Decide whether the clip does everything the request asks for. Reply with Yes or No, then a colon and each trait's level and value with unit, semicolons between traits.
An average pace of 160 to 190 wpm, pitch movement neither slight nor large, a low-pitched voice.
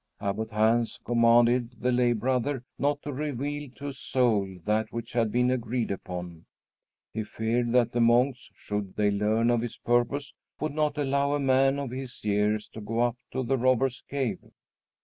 Yes: average, 175 wpm; average, 3.1 semitones; low, 120 Hz